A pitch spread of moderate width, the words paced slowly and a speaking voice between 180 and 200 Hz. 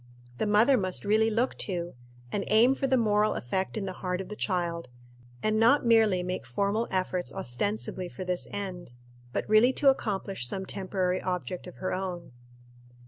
No: average, 3.1 semitones; average, 180 wpm; high, 190 Hz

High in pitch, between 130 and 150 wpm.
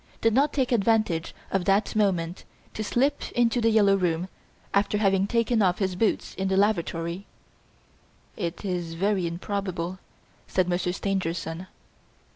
Yes: high, 195 Hz; average, 140 wpm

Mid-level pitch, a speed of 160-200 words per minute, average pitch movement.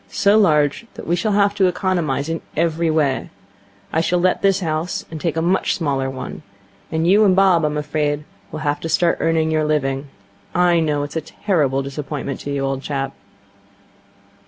Yes: medium, 160 Hz; average, 185 wpm; average, 3.4 semitones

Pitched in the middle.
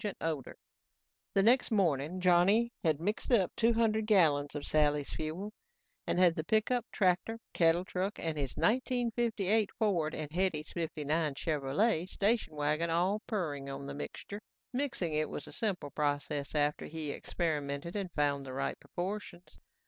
Yes: medium, 170 Hz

